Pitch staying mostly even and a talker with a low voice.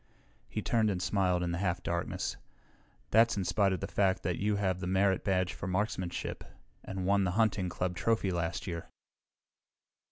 Yes: narrow, 2.1 semitones; very low, 95 Hz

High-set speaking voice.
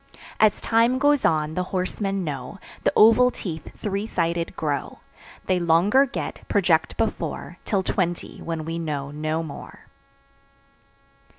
No: medium, 175 Hz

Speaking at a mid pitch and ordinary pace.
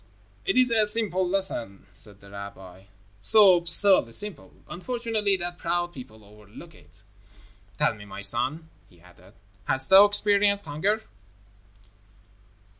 No: medium, 175 Hz; slow, 125 wpm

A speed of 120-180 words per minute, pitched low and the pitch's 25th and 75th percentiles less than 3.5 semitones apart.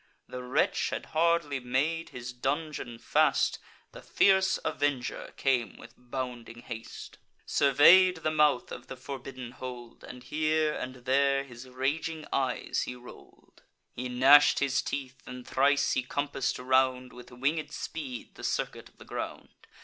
Yes: average, 145 wpm; low, 130 Hz; average, 2.7 semitones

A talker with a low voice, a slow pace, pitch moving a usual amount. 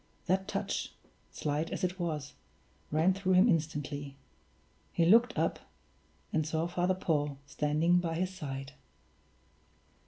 No: medium, 165 Hz; slow, 125 wpm; average, 3.7 semitones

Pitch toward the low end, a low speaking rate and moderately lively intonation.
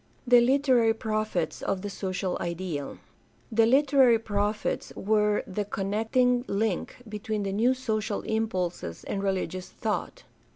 No: high, 215 Hz; slow, 130 wpm; average, 3.1 semitones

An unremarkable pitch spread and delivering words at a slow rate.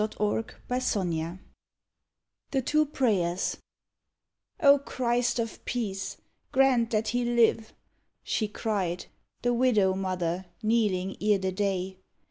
Yes: average, 4.3 semitones; slow, 120 wpm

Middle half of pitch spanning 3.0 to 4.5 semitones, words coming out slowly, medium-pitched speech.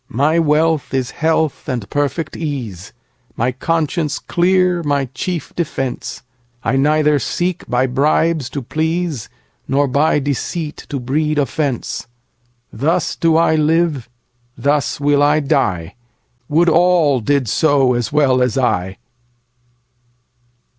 Yes: average, 4.1 semitones; slow, 105 wpm; medium, 145 Hz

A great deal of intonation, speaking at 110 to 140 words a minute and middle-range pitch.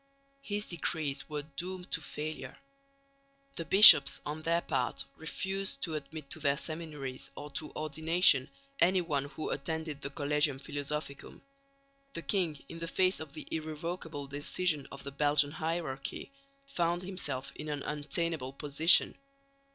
No: average, 2.8 semitones; slow, 135 wpm; medium, 155 Hz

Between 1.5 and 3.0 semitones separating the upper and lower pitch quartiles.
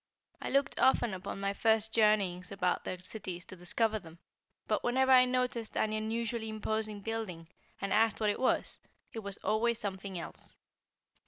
Yes: average, 2.7 semitones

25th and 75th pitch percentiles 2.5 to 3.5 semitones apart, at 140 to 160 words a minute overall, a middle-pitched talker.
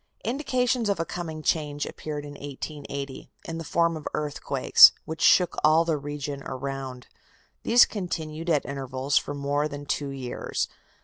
Yes: average, 2.9 semitones; average, 150 wpm; medium, 150 Hz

